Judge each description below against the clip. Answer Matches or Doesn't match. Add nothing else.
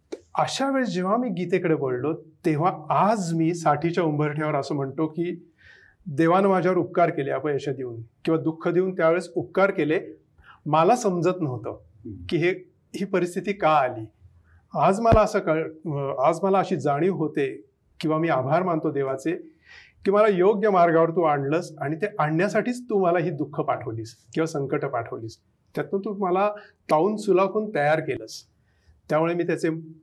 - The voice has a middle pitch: Matches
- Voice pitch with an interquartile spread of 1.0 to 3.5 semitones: Doesn't match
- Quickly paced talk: Matches